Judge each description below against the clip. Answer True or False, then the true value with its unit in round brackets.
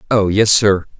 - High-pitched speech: False (100 Hz)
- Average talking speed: True (180 wpm)